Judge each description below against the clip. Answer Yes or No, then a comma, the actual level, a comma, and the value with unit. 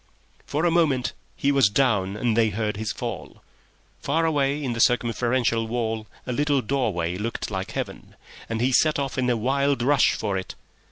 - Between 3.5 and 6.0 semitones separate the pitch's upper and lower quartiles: Yes, average, 4.0 semitones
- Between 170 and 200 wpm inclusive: Yes, average, 180 wpm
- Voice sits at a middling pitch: No, low, 120 Hz